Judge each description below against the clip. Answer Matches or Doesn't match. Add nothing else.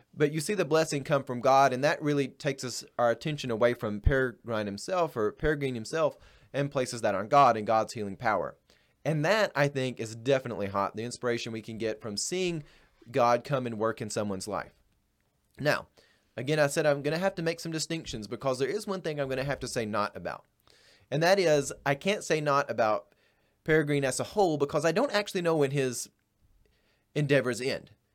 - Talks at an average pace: Doesn't match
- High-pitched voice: Doesn't match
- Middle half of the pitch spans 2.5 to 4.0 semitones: Doesn't match